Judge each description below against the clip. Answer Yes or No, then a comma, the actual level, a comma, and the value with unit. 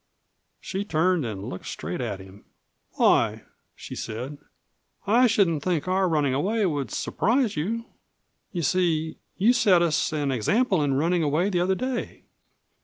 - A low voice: No, medium, 170 Hz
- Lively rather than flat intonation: Yes, wide, 5.7 semitones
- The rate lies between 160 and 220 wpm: No, average, 150 wpm